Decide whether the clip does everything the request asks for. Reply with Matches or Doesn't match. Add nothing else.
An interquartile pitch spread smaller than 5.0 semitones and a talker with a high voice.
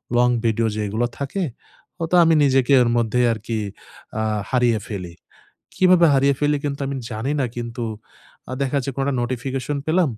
Doesn't match